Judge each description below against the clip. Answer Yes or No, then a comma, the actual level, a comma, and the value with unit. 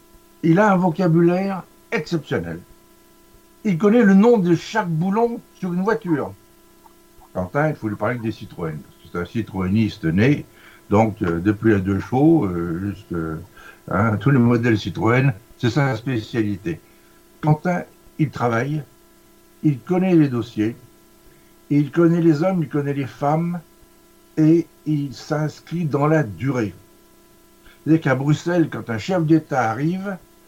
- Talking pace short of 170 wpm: Yes, slow, 145 wpm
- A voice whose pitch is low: No, medium, 150 Hz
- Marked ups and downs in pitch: Yes, wide, 7.1 semitones